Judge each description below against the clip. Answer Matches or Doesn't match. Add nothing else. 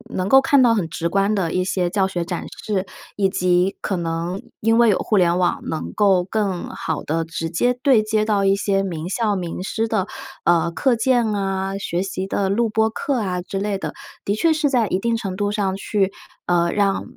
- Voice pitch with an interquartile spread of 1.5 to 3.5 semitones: Matches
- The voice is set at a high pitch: Matches